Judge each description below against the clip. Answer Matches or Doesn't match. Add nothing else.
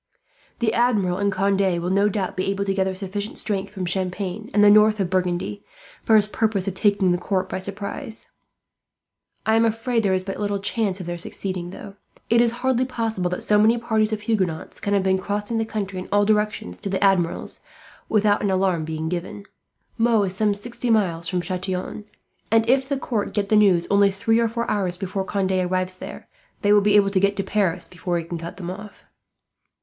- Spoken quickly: Matches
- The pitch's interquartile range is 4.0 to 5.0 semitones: Doesn't match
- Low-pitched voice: Doesn't match